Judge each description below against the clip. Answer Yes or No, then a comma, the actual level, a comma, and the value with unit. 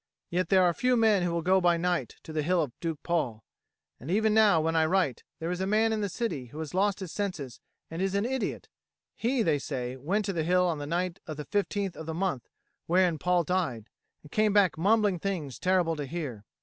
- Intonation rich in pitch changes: No, average, 3.9 semitones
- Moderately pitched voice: Yes, medium, 175 Hz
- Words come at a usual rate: No, fast, 235 wpm